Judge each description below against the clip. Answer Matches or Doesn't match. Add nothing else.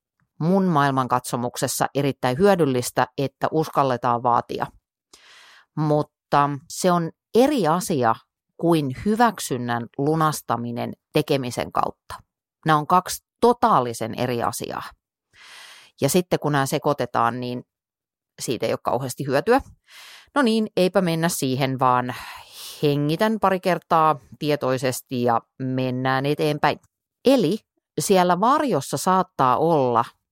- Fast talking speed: Doesn't match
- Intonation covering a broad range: Matches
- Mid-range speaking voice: Matches